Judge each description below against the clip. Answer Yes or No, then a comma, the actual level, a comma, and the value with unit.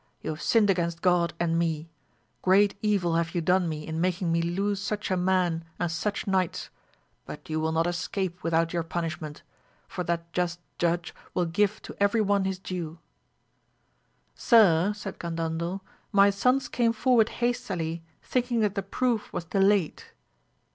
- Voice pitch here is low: No, medium, 180 Hz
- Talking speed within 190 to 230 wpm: No, average, 160 wpm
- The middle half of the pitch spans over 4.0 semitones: No, average, 3.3 semitones